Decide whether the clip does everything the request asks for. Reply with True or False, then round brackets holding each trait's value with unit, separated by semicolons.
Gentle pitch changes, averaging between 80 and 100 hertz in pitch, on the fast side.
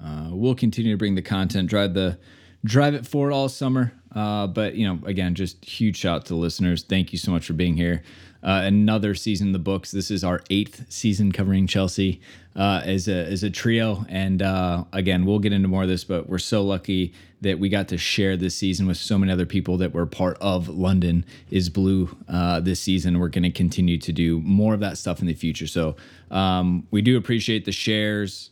True (2.3 semitones; 95 Hz; 225 wpm)